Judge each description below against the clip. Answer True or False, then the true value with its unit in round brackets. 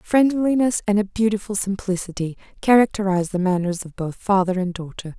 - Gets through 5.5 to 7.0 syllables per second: True (5.6 syllables/s)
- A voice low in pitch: False (195 Hz)